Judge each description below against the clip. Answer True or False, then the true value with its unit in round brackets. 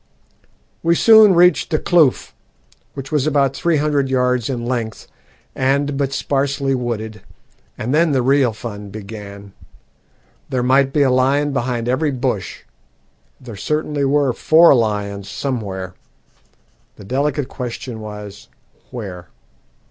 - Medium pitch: False (130 Hz)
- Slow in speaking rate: True (125 wpm)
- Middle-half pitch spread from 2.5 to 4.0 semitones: False (4.4 semitones)